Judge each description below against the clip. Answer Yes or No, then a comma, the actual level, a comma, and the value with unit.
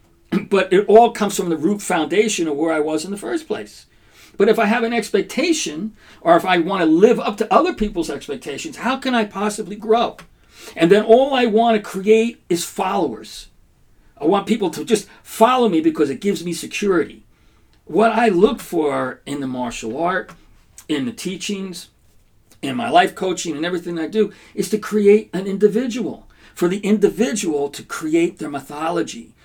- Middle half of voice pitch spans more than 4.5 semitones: Yes, average, 5.2 semitones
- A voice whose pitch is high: Yes, high, 200 Hz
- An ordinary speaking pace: Yes, average, 185 wpm